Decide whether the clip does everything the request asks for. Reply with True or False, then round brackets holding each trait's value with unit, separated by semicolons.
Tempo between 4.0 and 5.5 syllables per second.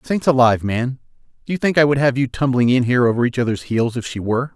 False (6.8 syllables/s)